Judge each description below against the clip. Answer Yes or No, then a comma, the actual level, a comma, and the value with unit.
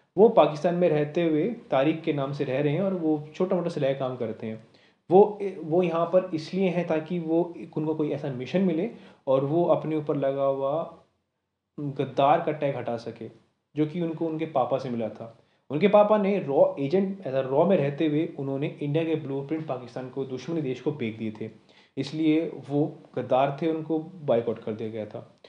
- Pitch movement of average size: Yes, average, 3.9 semitones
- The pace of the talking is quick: Yes, fast, 200 wpm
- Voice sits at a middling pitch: Yes, medium, 150 Hz